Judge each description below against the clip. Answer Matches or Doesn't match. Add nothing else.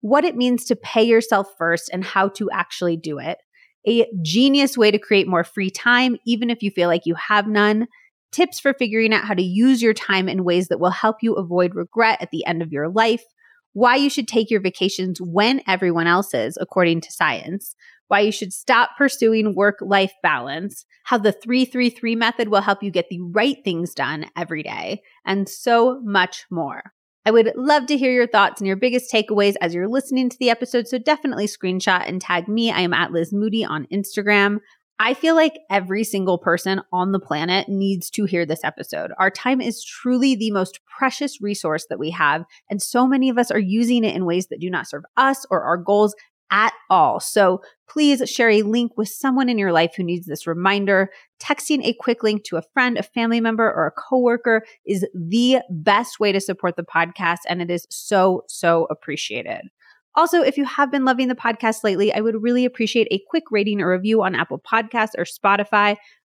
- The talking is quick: Matches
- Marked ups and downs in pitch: Doesn't match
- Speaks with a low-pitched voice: Doesn't match